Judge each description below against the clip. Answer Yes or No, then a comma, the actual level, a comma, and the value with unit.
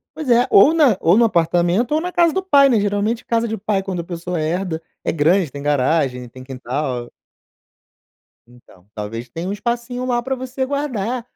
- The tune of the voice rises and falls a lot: Yes, wide, 8.0 semitones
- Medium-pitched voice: No, high, 195 Hz